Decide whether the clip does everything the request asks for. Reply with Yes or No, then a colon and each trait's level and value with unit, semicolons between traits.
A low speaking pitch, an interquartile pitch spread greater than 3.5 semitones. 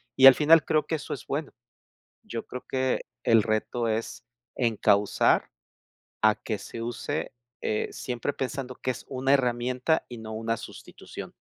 No: low, 125 Hz; average, 2.9 semitones